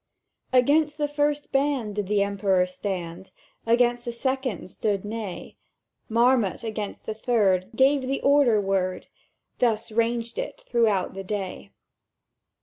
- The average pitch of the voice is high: Yes, high, 225 Hz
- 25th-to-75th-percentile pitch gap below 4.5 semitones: No, average, 4.8 semitones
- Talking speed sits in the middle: No, slow, 130 wpm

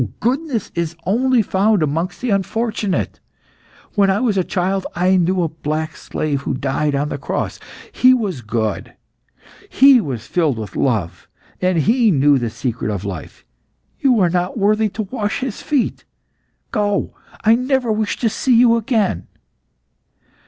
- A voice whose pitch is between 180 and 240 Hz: Yes, high, 190 Hz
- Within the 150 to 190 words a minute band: Yes, average, 155 wpm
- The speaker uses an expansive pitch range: Yes, wide, 7.4 semitones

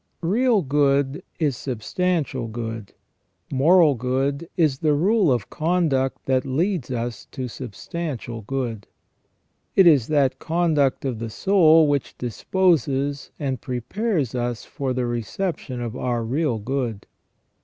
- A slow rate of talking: Yes, slow, 125 wpm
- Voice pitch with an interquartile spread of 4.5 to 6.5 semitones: Yes, average, 5.0 semitones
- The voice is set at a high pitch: No, low, 135 Hz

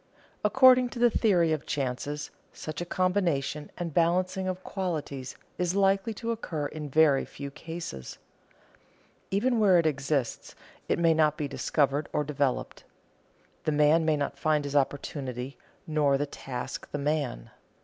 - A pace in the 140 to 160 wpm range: Yes, average, 150 wpm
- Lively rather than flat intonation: No, average, 4.4 semitones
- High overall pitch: No, medium, 155 Hz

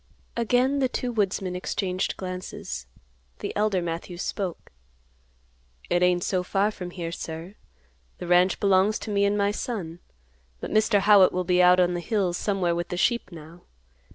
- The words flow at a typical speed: Yes, average, 165 wpm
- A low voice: No, medium, 185 Hz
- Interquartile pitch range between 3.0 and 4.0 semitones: No, narrow, 2.6 semitones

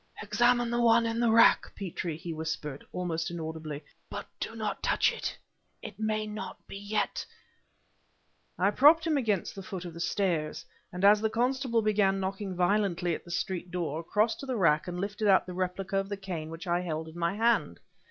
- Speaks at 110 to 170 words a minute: No, average, 200 wpm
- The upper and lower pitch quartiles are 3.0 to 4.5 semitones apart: Yes, average, 4.1 semitones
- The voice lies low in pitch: No, high, 195 Hz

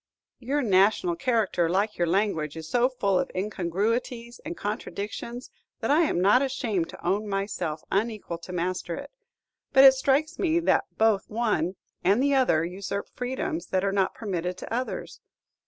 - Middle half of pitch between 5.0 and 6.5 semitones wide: Yes, wide, 5.4 semitones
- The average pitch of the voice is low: No, high, 210 Hz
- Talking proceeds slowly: No, average, 165 wpm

